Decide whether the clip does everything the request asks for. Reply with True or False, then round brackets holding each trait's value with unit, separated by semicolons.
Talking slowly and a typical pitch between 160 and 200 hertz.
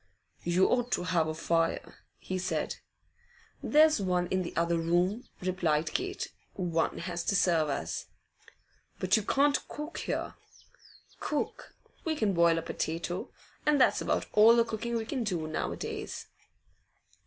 False (155 wpm; 185 Hz)